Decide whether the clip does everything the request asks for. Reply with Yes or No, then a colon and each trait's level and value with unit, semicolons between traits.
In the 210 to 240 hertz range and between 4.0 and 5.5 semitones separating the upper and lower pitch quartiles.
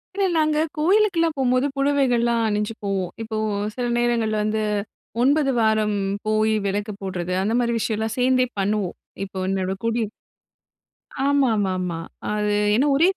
Yes: high, 225 Hz; average, 4.3 semitones